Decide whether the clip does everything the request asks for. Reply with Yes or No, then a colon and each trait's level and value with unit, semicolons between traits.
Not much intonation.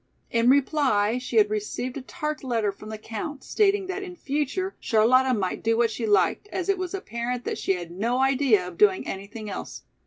No: wide, 5.6 semitones